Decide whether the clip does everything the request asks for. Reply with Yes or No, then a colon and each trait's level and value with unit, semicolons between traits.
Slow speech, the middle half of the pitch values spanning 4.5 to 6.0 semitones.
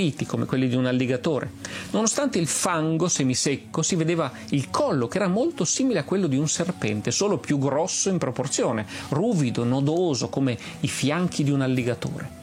No: fast, 170 wpm; average, 5.1 semitones